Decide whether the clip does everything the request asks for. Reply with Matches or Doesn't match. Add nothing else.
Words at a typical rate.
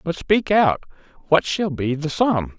Matches